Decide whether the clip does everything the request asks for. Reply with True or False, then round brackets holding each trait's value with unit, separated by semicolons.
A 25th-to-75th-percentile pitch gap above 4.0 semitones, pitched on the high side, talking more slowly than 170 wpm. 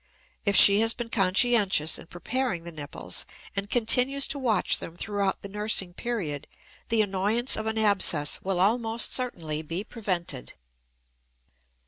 True (4.6 semitones; 200 Hz; 140 wpm)